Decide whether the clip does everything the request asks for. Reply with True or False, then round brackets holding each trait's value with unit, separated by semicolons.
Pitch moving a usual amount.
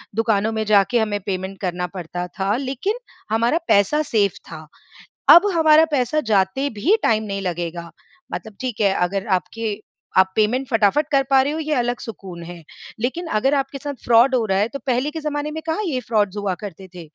False (5.9 semitones)